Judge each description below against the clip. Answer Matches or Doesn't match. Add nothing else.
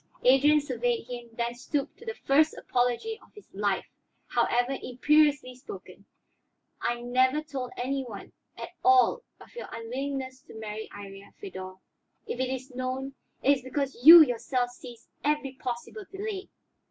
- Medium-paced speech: Matches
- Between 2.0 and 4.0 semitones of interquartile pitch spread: Matches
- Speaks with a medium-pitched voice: Doesn't match